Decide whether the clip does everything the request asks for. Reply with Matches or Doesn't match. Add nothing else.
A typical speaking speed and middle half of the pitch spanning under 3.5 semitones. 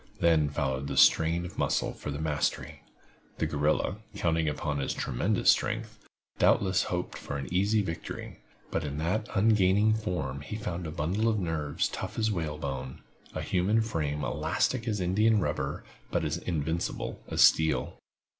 Doesn't match